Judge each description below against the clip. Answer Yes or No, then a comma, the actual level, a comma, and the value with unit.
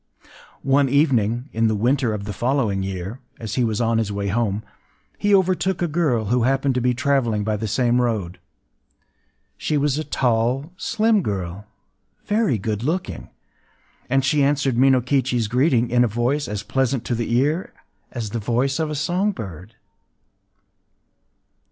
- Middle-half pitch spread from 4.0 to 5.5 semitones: Yes, average, 4.3 semitones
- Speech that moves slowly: No, average, 160 wpm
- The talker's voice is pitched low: Yes, low, 125 Hz